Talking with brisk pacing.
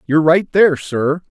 No: average, 175 wpm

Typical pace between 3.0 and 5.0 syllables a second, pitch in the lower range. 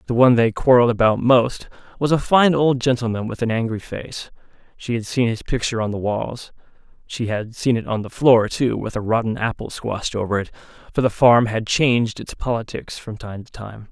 No: 5.4 syllables/s; low, 115 Hz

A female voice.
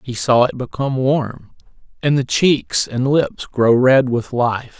No: male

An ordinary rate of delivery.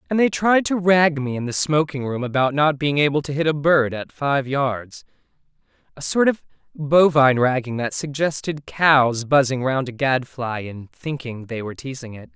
Yes: average, 190 wpm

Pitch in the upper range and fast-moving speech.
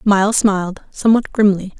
No: high, 200 Hz; slow, 135 wpm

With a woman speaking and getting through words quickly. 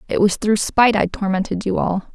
Yes: female; fast, 225 wpm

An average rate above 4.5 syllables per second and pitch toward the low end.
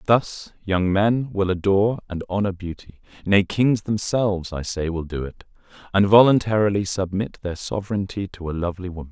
Yes: 5.3 syllables/s; very low, 95 Hz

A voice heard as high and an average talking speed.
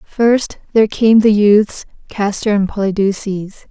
No: high, 210 Hz; slow, 130 wpm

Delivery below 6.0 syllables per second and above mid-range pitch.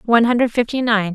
No: 6.3 syllables/s; high, 230 Hz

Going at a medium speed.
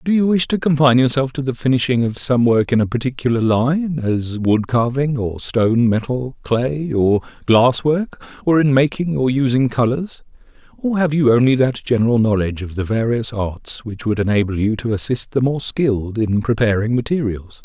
Yes: average, 185 wpm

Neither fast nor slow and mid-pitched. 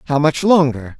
Yes: average, 180 wpm; medium, 145 Hz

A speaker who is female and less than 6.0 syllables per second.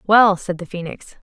Yes: female; 4.5 syllables/s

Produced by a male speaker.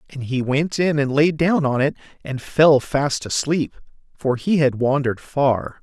Yes: male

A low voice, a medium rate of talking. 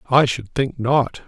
Yes: low, 130 Hz; average, 190 wpm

